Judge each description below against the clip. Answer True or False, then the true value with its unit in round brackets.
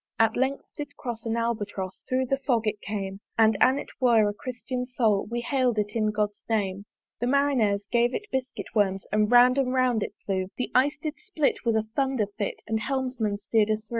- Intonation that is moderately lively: True (3.5 semitones)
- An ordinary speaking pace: False (210 wpm)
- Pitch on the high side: True (230 Hz)